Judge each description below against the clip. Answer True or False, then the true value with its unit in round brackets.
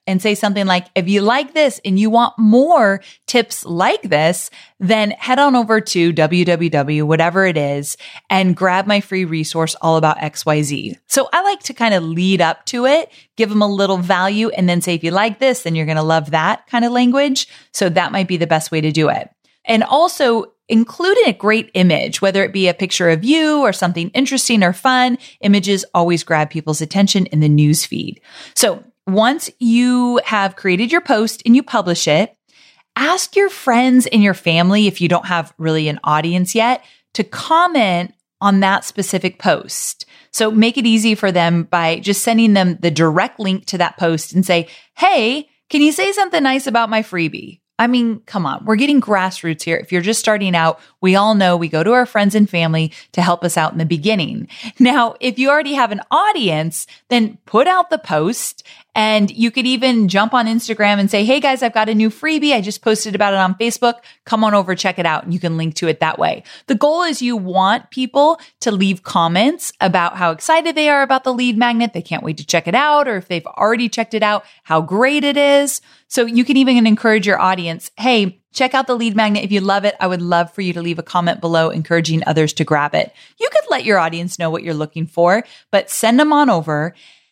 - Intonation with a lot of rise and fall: True (5.9 semitones)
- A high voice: True (205 Hz)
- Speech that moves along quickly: True (220 wpm)